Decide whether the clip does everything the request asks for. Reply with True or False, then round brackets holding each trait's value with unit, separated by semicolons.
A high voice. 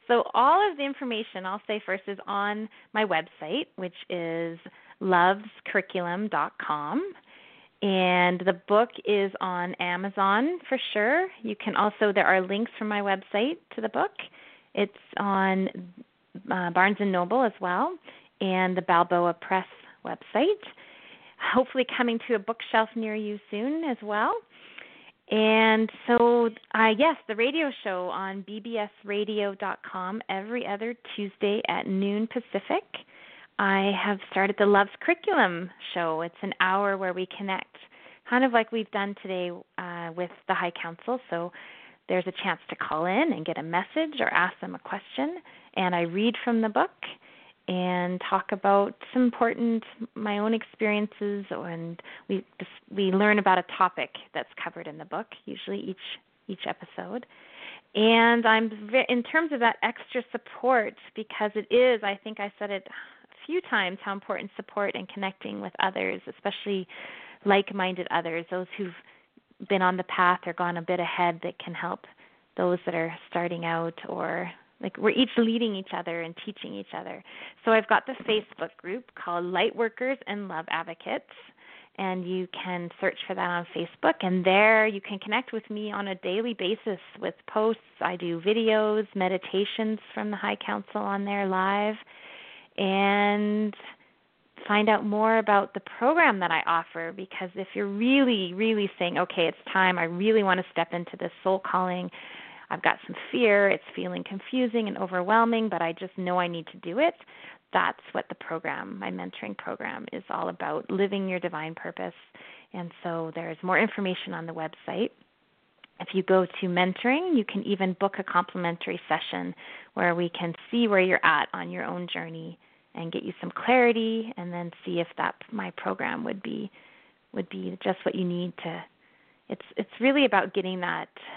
True (200 Hz)